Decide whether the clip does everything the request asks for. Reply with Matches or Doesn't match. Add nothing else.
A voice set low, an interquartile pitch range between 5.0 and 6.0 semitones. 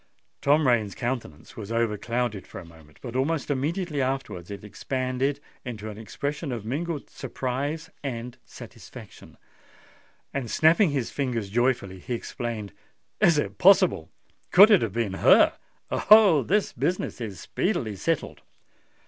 Matches